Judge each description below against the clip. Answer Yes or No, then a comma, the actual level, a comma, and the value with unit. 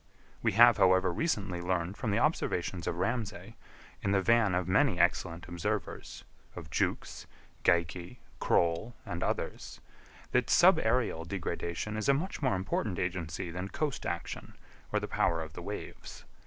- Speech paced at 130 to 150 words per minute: Yes, average, 145 wpm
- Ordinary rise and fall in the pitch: Yes, average, 4.6 semitones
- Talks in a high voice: No, very low, 95 Hz